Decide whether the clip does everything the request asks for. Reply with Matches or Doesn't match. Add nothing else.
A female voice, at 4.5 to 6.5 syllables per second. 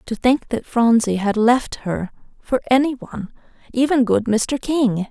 Doesn't match